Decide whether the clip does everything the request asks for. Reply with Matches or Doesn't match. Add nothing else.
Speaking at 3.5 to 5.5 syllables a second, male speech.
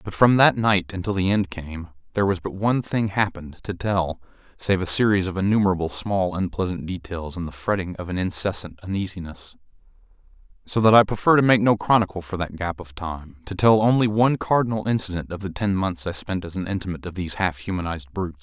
Doesn't match